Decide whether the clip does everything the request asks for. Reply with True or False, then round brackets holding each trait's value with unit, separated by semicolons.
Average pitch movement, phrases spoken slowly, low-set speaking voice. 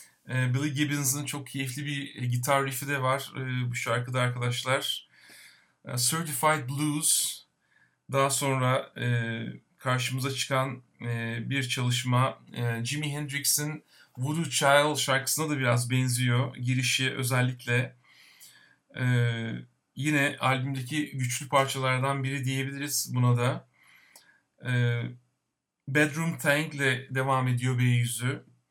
False (2.2 semitones; 90 wpm; 130 Hz)